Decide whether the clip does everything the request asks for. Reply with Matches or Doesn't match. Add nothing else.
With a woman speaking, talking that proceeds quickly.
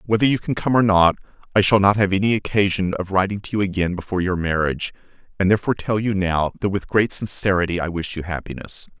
Doesn't match